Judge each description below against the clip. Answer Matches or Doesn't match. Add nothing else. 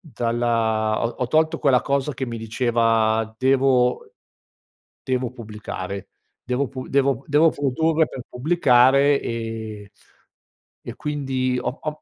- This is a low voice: Matches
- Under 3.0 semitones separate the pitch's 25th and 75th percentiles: Doesn't match